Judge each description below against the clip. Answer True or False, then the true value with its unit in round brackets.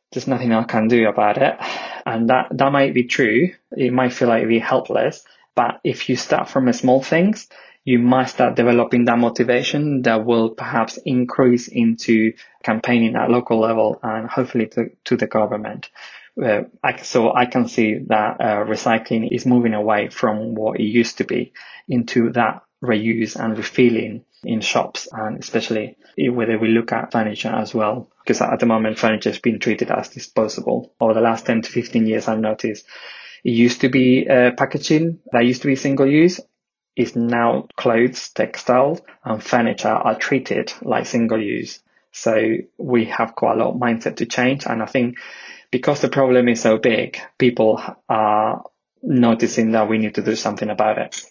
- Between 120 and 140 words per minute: False (180 wpm)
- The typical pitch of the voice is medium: False (120 Hz)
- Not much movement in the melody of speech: True (2.2 semitones)